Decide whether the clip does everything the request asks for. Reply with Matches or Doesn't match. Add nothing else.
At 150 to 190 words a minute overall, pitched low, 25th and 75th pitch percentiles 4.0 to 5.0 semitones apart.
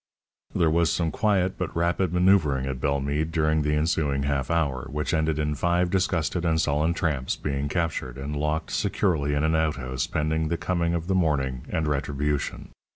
Doesn't match